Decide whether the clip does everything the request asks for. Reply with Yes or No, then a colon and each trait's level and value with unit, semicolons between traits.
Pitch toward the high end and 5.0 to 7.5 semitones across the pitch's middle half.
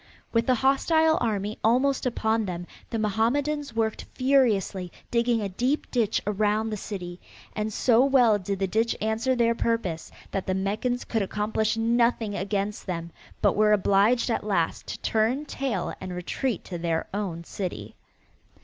No: high, 220 Hz; average, 3.5 semitones